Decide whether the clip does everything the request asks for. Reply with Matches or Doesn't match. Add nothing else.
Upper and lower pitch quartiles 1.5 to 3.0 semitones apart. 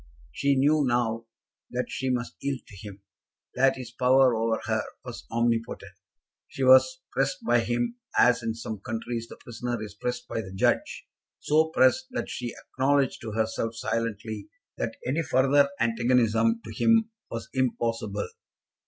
Matches